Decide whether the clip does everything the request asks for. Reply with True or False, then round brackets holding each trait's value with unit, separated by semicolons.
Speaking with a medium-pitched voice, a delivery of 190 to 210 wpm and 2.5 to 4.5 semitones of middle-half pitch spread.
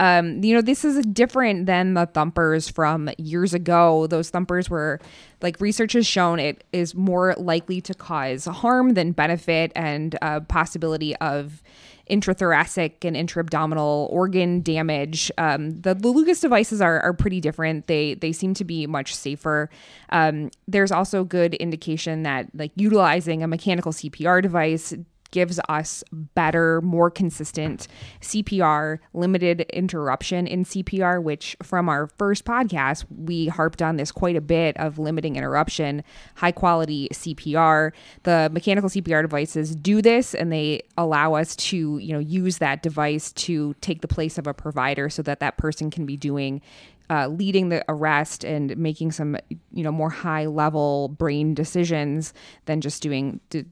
False (160 Hz; 160 wpm; 2.8 semitones)